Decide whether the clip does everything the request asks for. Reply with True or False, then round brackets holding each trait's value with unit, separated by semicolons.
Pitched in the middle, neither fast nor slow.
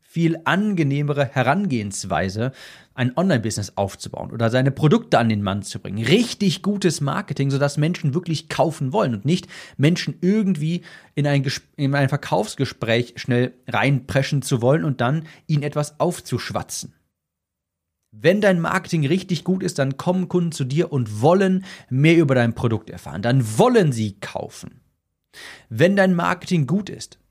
True (145 Hz; 155 wpm)